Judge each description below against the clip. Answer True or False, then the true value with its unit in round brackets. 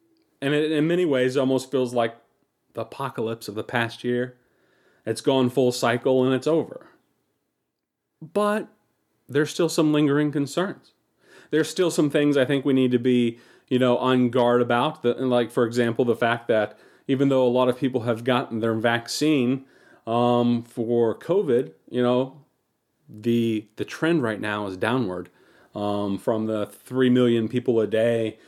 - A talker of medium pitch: False (125 Hz)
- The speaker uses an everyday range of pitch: True (3.1 semitones)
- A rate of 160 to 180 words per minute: True (170 wpm)